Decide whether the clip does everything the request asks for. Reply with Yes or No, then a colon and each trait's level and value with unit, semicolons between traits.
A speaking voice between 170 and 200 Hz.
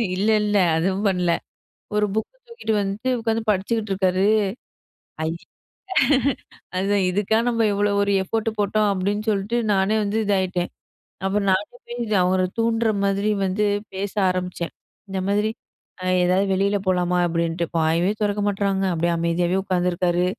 Yes: high, 195 Hz